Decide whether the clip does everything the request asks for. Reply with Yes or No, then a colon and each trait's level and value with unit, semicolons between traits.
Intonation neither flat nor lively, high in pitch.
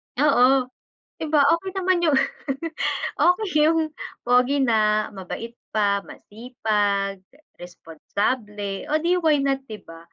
No: wide, 6.6 semitones; very high, 250 Hz